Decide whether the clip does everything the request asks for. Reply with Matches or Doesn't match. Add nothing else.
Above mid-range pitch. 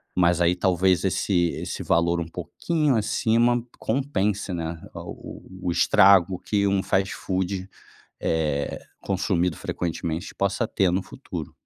Doesn't match